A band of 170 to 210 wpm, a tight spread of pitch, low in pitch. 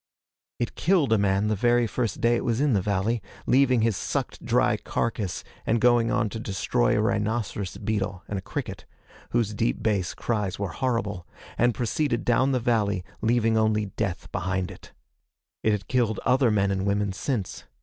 No: average, 180 wpm; average, 3.0 semitones; low, 110 Hz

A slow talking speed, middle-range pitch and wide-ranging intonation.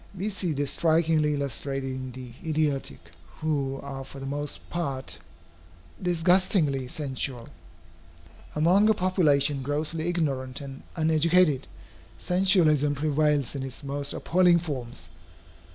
No: slow, 115 wpm; medium, 145 Hz; average, 3.5 semitones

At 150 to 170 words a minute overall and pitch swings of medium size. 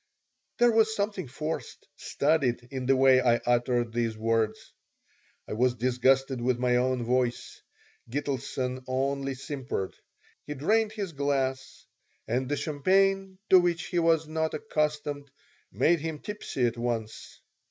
No: slow, 135 wpm; average, 4.4 semitones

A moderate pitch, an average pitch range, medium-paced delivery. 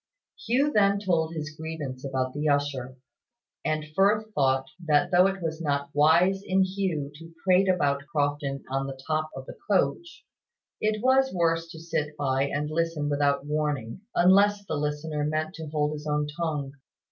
Yes: medium, 155 Hz; average, 4.1 semitones; average, 170 wpm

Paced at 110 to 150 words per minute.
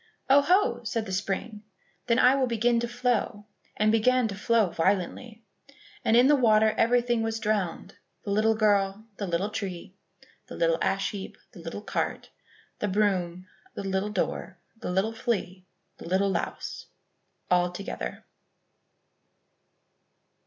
Yes: average, 140 wpm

